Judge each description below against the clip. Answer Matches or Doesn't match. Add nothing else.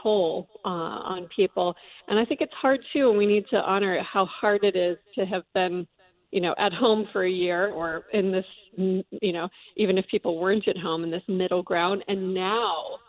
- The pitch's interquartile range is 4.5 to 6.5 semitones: Doesn't match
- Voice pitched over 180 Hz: Matches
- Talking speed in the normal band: Doesn't match